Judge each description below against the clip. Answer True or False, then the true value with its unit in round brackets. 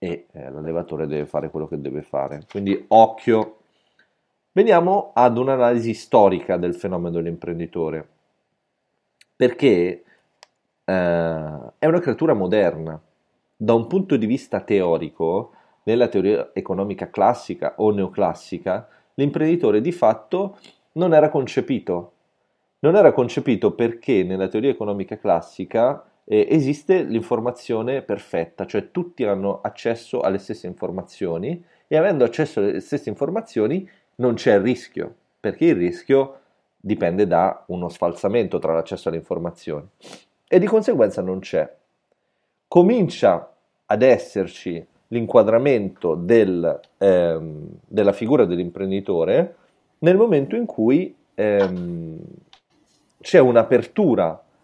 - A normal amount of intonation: False (7.6 semitones)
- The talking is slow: True (110 wpm)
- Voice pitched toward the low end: True (105 Hz)